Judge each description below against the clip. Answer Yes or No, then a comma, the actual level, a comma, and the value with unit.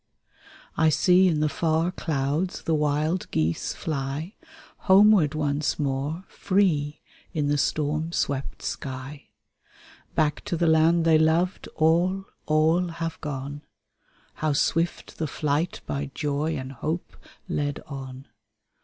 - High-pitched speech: No, medium, 155 Hz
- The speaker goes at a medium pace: No, slow, 125 wpm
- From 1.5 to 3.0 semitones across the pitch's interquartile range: Yes, narrow, 2.6 semitones